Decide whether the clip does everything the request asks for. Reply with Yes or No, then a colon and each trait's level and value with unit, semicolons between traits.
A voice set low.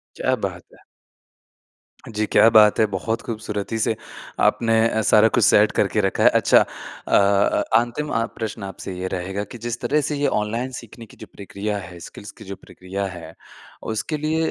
Yes: low, 105 Hz